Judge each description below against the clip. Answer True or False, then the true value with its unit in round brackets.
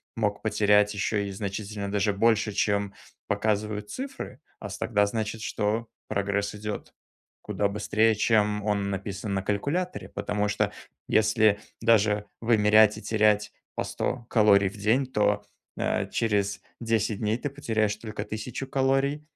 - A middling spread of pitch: False (1.6 semitones)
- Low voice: True (105 Hz)